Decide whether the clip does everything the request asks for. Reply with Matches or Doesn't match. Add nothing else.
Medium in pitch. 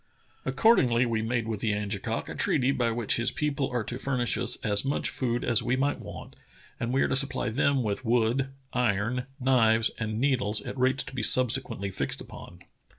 Doesn't match